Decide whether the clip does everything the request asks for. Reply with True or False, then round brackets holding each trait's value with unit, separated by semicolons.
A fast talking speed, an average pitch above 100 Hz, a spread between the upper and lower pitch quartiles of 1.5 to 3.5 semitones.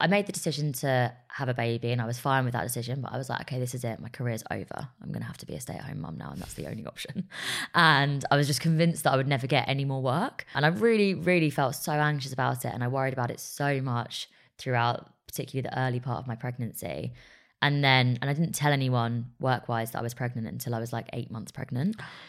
True (270 wpm; 130 Hz; 3.2 semitones)